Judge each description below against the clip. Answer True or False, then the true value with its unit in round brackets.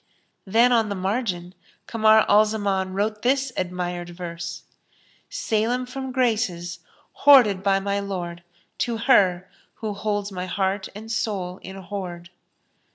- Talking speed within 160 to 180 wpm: False (135 wpm)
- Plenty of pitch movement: False (3.6 semitones)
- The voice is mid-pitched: False (200 Hz)